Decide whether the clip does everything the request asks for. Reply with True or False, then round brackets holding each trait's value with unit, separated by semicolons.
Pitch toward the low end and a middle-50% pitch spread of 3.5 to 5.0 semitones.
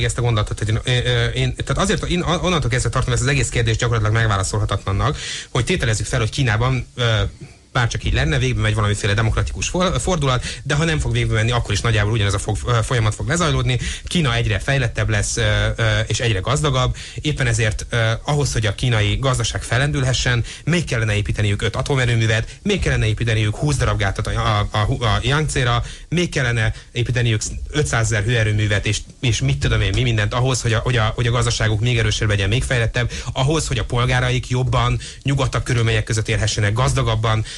False (120 Hz; 2.9 semitones)